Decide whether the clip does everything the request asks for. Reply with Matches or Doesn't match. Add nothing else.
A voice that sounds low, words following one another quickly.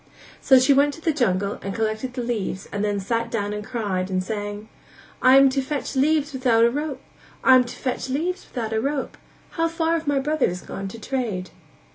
Doesn't match